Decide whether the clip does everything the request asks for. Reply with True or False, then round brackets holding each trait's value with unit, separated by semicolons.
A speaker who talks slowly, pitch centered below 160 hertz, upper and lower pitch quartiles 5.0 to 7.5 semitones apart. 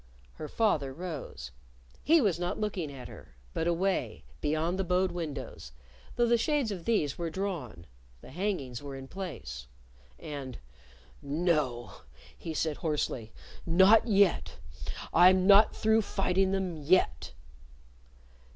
False (130 wpm; 170 Hz; 5.4 semitones)